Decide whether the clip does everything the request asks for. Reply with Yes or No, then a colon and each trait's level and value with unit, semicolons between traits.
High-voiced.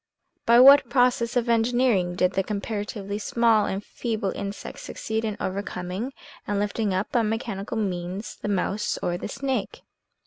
Yes: high, 210 Hz